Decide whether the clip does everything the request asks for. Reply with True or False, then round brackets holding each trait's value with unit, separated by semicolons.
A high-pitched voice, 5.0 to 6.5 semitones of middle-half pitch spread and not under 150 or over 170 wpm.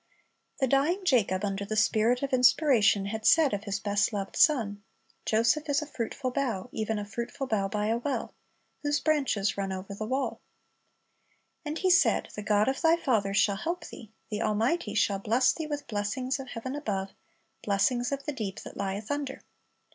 False (230 Hz; 5.3 semitones; 185 wpm)